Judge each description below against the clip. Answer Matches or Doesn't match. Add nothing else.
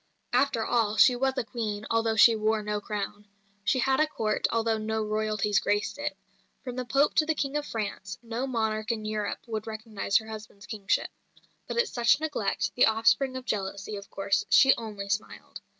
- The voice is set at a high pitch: Matches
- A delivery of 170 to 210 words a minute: Matches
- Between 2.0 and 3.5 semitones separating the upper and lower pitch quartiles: Matches